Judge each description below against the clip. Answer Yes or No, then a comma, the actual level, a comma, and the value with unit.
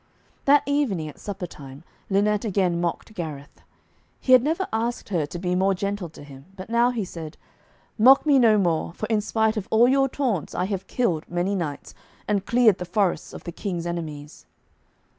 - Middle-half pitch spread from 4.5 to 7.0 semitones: Yes, average, 5.0 semitones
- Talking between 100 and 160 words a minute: No, average, 190 wpm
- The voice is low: No, high, 195 Hz